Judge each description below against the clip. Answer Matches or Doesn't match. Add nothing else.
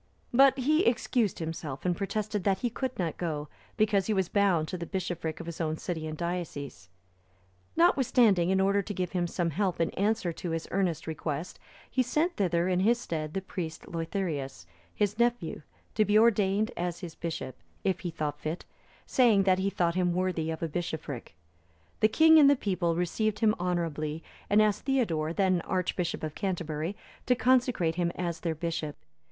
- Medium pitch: Matches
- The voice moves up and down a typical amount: Matches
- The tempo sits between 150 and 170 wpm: Doesn't match